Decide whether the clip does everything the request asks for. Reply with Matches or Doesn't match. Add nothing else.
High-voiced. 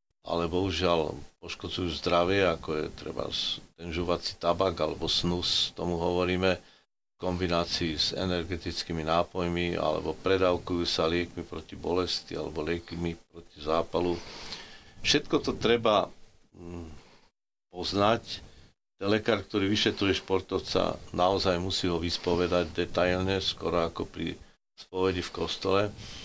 Doesn't match